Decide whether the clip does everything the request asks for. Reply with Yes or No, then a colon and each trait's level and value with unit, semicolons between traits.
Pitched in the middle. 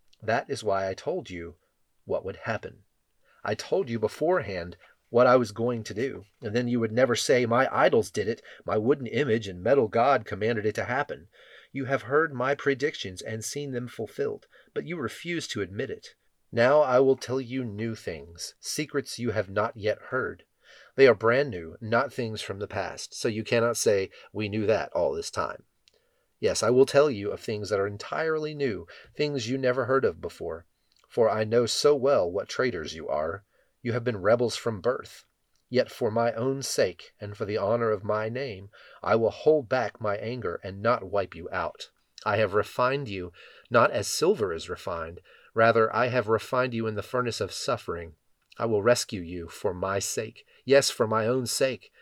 No: low, 120 Hz